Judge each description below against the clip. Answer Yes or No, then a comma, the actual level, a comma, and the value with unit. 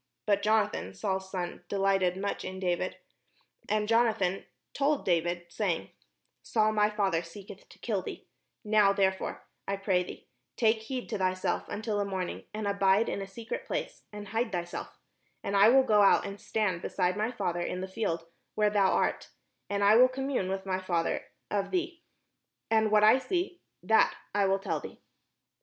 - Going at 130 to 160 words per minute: No, average, 180 wpm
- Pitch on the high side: Yes, high, 200 Hz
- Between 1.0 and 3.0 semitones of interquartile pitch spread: Yes, narrow, 2.5 semitones